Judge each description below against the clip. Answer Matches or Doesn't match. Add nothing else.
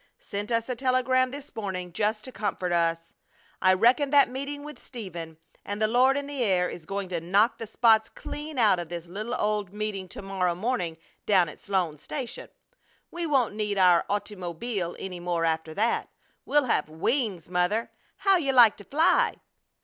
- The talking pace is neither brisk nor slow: Matches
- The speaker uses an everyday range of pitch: Doesn't match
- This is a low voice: Doesn't match